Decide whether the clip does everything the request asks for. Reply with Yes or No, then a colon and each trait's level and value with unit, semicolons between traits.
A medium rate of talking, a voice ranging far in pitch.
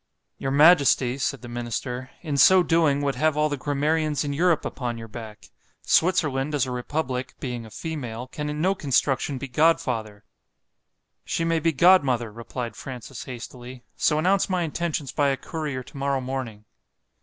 No: average, 155 wpm; average, 3.8 semitones